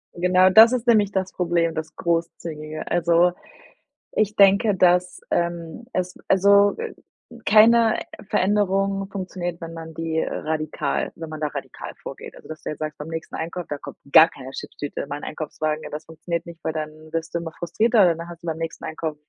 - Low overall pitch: No, medium, 170 Hz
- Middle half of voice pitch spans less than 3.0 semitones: No, average, 3.3 semitones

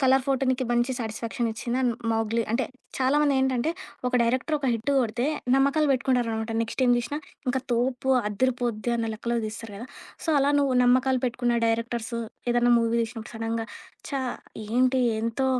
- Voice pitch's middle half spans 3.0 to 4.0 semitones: No, narrow, 2.4 semitones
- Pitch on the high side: Yes, high, 245 Hz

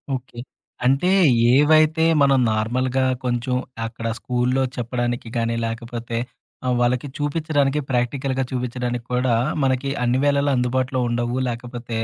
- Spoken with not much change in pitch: Yes, narrow, 1.9 semitones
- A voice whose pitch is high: No, low, 125 Hz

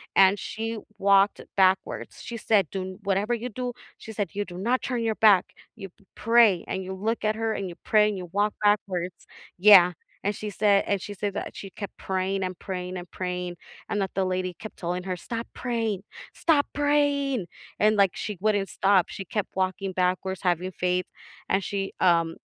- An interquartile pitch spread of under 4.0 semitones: Yes, narrow, 2.5 semitones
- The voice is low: No, high, 195 Hz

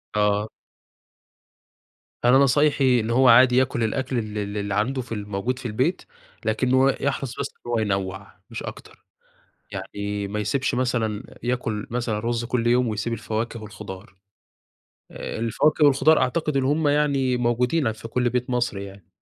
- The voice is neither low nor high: No, low, 120 Hz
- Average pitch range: Yes, average, 3.6 semitones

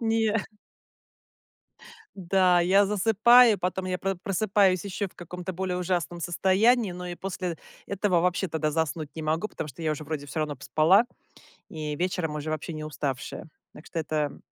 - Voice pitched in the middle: Yes, medium, 180 Hz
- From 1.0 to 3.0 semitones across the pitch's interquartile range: No, average, 3.7 semitones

